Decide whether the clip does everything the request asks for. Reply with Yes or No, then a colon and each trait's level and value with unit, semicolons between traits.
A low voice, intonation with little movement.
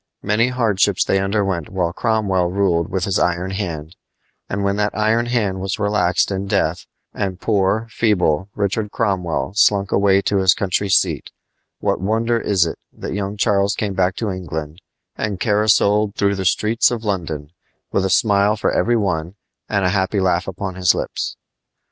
Yes: low, 100 Hz; narrow, 2.2 semitones